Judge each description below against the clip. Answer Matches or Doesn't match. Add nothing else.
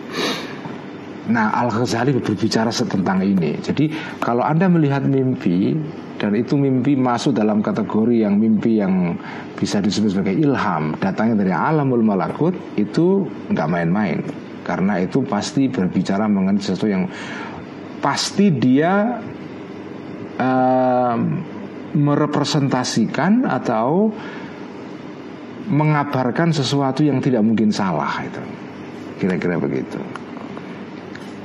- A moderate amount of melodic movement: Matches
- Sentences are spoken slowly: Doesn't match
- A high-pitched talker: Doesn't match